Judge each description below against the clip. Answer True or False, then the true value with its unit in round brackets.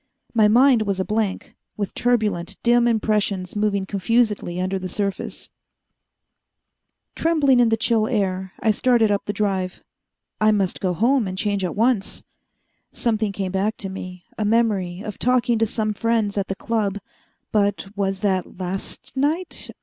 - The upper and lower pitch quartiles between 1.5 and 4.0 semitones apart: True (2.9 semitones)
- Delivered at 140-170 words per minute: True (155 wpm)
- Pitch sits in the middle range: False (210 Hz)